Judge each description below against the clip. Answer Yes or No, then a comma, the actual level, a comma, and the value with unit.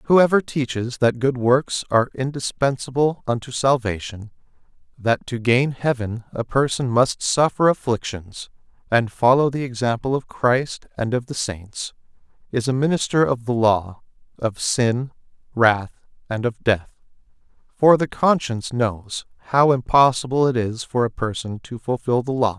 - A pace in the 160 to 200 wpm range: No, average, 145 wpm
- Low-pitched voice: Yes, low, 125 Hz